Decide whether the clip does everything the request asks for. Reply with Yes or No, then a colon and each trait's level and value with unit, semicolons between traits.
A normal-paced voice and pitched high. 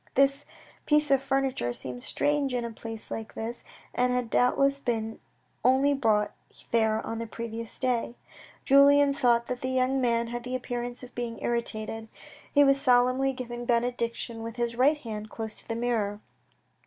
Yes: average, 170 wpm; high, 240 Hz